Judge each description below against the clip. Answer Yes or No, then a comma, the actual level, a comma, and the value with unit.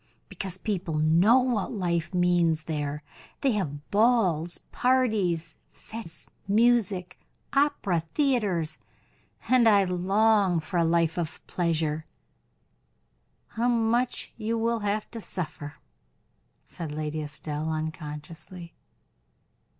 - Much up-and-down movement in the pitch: Yes, wide, 5.7 semitones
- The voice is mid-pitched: Yes, medium, 180 Hz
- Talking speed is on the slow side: Yes, slow, 105 wpm